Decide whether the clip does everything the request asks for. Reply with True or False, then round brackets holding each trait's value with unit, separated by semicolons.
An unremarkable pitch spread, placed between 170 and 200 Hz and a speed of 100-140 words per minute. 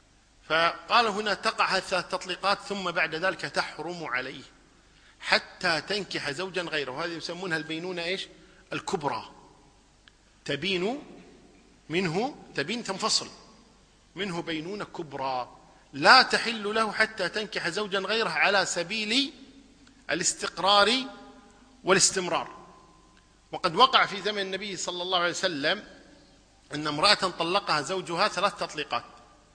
True (3.5 semitones; 185 Hz; 110 wpm)